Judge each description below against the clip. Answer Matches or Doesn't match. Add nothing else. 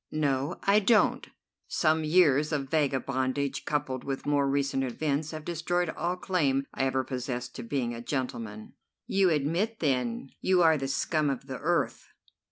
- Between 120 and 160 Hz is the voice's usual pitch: Matches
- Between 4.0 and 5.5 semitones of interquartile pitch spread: Doesn't match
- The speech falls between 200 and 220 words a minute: Doesn't match